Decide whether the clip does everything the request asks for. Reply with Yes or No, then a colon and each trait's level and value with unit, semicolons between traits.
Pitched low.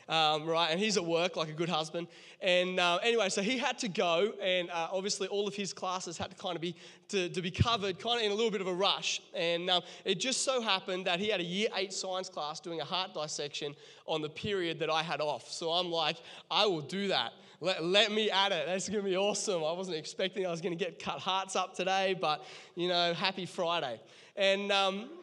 No: medium, 185 Hz